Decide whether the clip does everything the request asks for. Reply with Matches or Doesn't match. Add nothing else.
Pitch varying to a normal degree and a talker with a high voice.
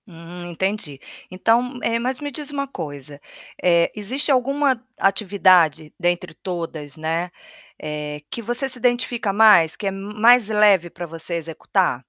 Doesn't match